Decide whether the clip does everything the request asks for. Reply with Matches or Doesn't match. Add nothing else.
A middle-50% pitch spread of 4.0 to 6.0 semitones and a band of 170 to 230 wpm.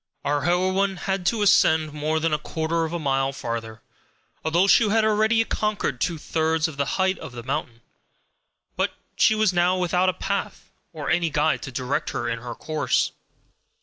Matches